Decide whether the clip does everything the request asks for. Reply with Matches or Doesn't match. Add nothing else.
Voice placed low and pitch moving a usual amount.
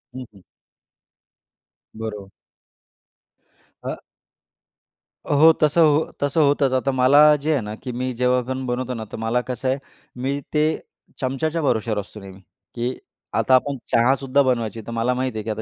Matches